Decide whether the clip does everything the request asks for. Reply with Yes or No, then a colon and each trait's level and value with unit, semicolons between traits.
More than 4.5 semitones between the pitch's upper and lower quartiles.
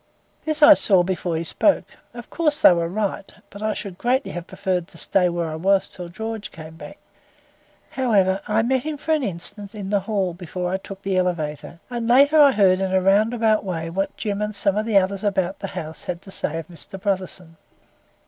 No: average, 3.6 semitones